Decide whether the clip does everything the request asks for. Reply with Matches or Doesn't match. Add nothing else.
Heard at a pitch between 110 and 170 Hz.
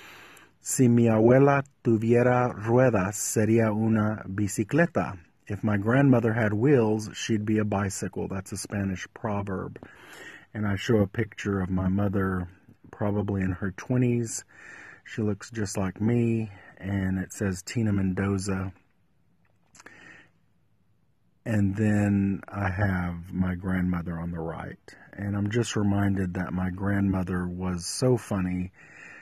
Doesn't match